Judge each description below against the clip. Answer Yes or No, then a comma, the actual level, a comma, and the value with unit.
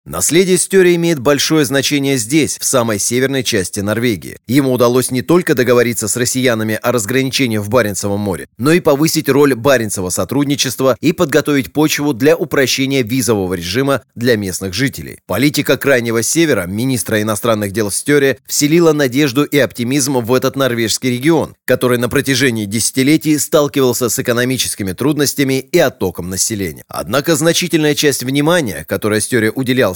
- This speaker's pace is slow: No, average, 145 wpm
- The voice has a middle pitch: No, low, 130 Hz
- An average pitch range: Yes, average, 4.3 semitones